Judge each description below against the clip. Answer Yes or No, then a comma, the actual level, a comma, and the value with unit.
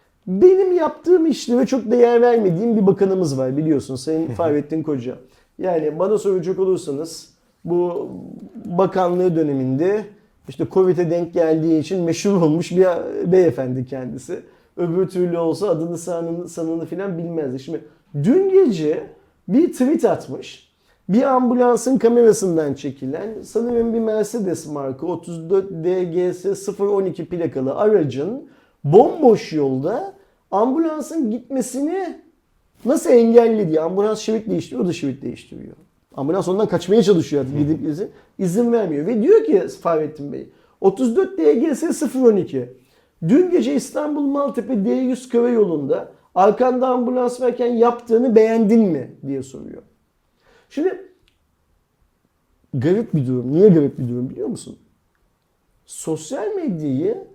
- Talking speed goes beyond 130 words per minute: No, average, 120 wpm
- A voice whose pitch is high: Yes, high, 195 Hz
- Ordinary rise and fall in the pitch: No, wide, 7.1 semitones